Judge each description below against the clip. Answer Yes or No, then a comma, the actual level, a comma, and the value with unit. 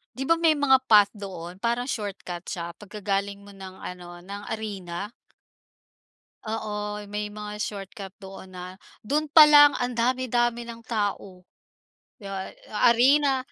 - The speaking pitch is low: No, high, 210 Hz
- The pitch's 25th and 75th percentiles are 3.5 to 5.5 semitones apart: Yes, average, 4.0 semitones